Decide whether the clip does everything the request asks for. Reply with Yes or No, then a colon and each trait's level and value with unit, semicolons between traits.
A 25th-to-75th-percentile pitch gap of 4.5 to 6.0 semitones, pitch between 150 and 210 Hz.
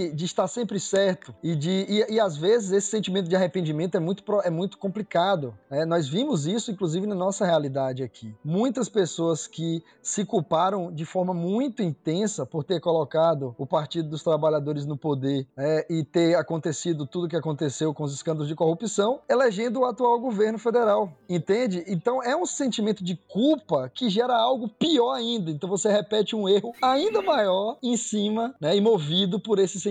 Yes: average, 5.1 semitones; high, 190 Hz